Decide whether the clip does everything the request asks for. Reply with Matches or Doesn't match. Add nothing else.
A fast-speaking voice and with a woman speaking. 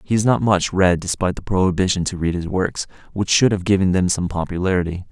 Doesn't match